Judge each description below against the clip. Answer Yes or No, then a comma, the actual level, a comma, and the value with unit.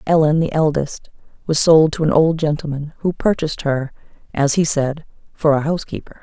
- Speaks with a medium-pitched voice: Yes, medium, 155 Hz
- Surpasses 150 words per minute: Yes, average, 175 wpm